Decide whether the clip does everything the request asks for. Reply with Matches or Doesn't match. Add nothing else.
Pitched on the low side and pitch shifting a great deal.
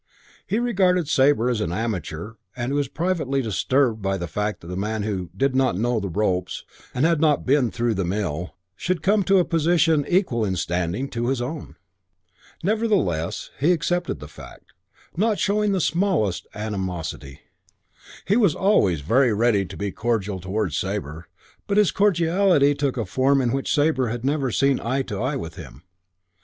Matches